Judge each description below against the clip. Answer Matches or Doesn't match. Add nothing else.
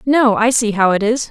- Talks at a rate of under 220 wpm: Doesn't match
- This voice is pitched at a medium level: Doesn't match